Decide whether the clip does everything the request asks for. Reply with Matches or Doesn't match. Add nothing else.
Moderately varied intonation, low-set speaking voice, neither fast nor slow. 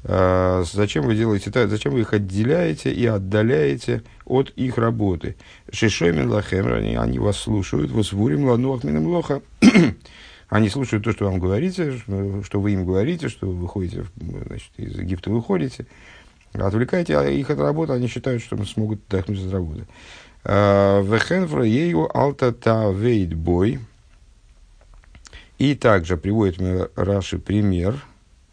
Matches